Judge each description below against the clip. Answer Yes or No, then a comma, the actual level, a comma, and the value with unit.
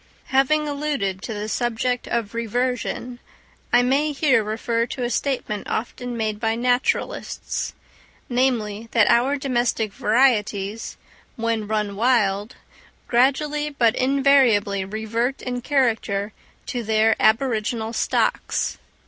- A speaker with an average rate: No, slow, 110 wpm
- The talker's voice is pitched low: No, high, 235 Hz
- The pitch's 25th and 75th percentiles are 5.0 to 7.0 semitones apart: No, average, 3.0 semitones